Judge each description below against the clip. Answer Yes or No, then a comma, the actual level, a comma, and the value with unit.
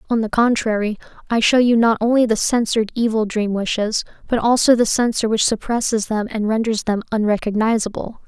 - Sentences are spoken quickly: No, average, 175 wpm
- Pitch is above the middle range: Yes, high, 220 Hz